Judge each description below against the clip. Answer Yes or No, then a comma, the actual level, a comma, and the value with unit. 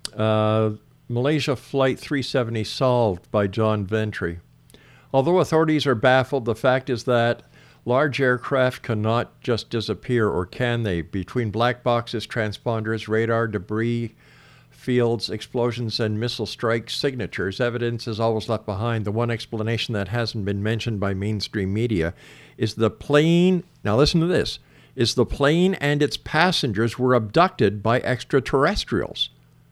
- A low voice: Yes, low, 120 Hz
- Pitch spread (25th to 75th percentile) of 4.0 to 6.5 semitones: No, average, 3.0 semitones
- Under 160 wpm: Yes, slow, 135 wpm